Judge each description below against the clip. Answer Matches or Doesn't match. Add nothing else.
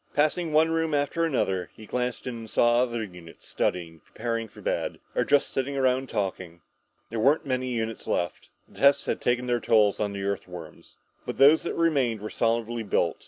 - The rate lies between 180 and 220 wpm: Matches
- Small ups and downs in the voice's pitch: Doesn't match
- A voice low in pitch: Matches